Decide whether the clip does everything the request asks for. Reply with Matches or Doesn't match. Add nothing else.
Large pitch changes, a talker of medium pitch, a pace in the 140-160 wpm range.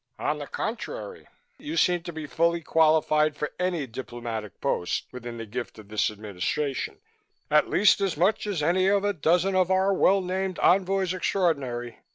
Doesn't match